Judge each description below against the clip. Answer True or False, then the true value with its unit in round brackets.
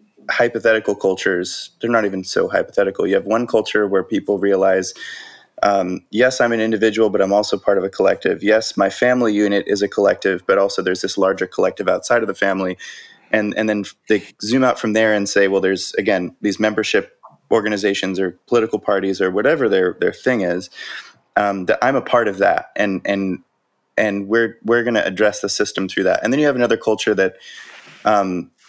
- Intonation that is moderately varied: False (2.2 semitones)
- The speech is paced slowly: False (200 wpm)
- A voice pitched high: False (105 Hz)